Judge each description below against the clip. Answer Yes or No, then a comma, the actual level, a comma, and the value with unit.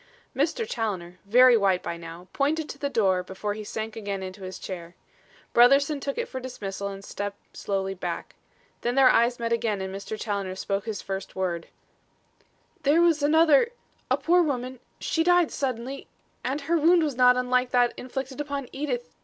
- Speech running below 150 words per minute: No, average, 180 wpm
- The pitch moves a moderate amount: No, wide, 6.2 semitones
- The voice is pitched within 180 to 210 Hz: No, high, 240 Hz